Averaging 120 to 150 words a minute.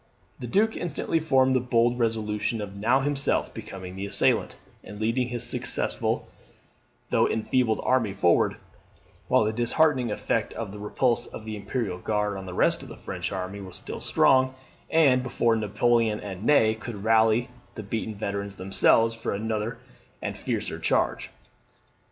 No: average, 160 wpm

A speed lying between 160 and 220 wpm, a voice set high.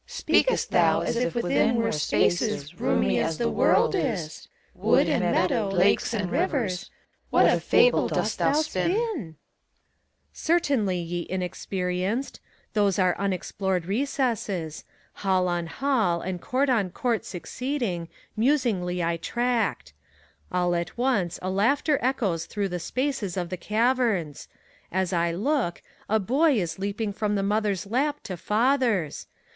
No: average, 145 wpm; high, 205 Hz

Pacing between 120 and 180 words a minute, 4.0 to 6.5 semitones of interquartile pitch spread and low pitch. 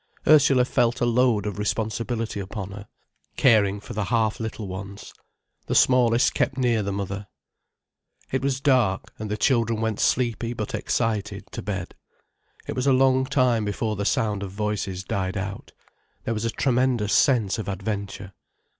No: average, 165 wpm; average, 3.3 semitones; low, 110 Hz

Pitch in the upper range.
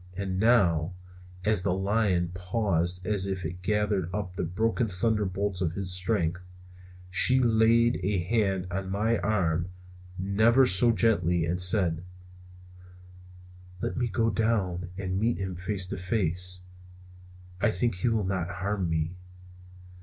No: very low, 95 Hz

